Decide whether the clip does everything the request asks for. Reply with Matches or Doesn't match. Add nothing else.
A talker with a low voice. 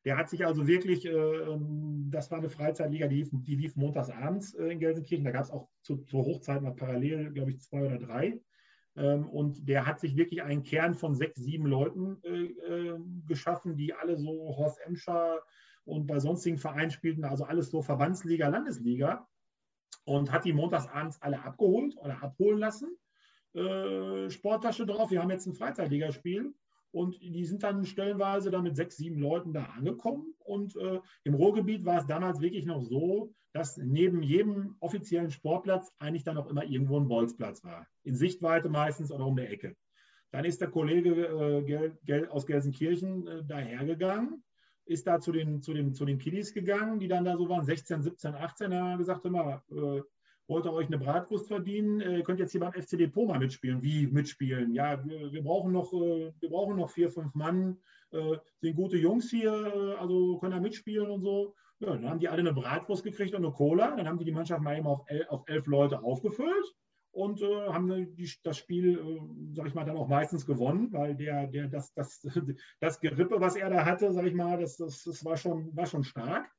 Doesn't match